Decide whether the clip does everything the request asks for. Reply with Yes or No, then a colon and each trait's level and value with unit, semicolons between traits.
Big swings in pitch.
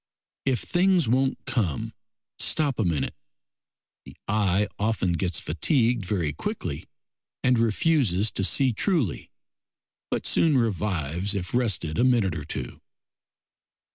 Yes: wide, 6.2 semitones